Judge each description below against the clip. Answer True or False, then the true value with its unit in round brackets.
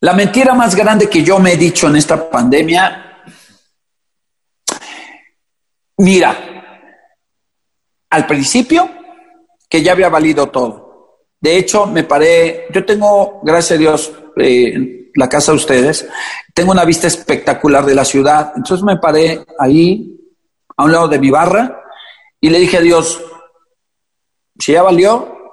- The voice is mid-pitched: True (170 Hz)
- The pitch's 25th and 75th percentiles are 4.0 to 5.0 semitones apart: True (4.7 semitones)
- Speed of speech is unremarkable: True (140 wpm)